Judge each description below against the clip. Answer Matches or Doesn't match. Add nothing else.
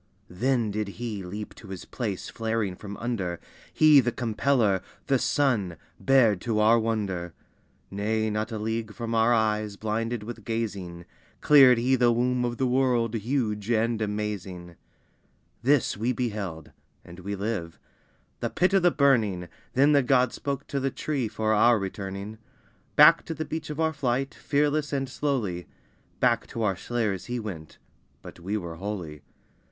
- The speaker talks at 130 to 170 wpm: Matches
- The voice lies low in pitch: Matches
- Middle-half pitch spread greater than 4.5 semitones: Doesn't match